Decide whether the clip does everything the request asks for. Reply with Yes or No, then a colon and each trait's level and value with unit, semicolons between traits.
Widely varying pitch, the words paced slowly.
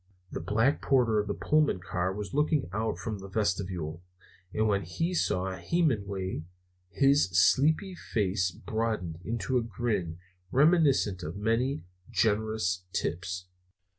Yes: wide, 5.8 semitones; slow, 130 wpm